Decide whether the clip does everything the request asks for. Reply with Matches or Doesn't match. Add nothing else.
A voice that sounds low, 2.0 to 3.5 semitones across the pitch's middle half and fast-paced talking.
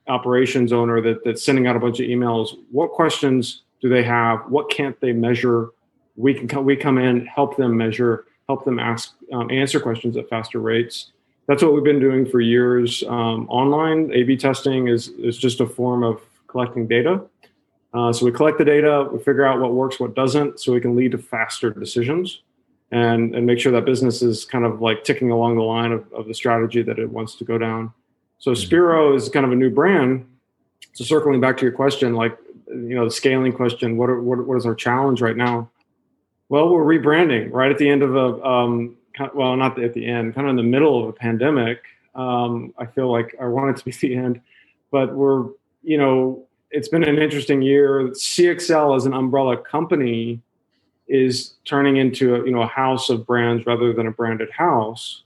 Matches